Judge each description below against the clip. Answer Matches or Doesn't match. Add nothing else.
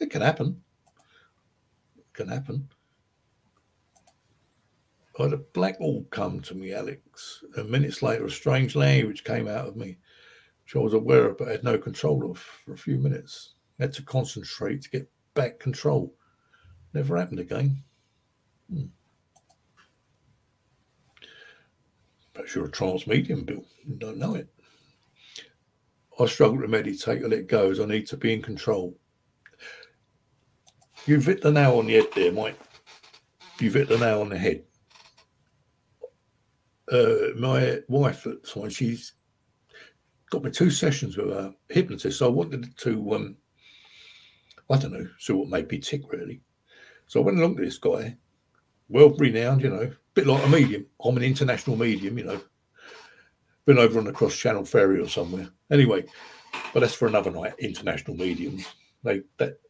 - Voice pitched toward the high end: Doesn't match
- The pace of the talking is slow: Doesn't match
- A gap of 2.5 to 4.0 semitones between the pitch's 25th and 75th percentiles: Doesn't match